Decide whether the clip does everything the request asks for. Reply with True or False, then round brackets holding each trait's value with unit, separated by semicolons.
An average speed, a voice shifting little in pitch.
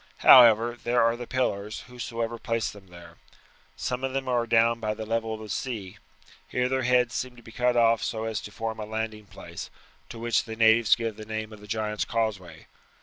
False (210 wpm; 1.7 semitones)